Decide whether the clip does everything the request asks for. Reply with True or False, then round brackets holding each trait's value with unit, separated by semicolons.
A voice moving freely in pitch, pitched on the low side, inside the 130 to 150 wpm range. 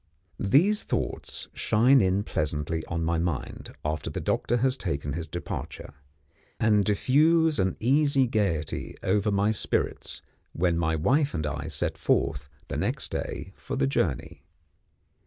True (8.1 semitones; 95 Hz; 140 wpm)